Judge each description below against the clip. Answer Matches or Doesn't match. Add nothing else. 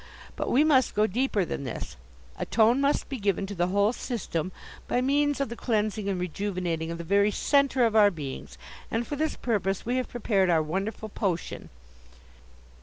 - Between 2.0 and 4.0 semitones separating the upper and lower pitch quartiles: Doesn't match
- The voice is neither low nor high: Doesn't match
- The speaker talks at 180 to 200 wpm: Matches